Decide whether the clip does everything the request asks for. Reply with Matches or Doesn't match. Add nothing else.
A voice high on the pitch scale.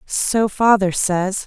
Matches